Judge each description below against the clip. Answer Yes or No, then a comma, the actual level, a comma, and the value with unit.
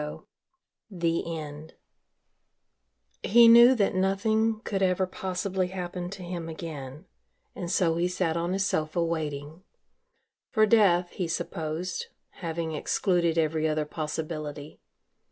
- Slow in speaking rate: Yes, slow, 120 wpm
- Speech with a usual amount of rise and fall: Yes, average, 3.1 semitones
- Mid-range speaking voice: Yes, medium, 175 Hz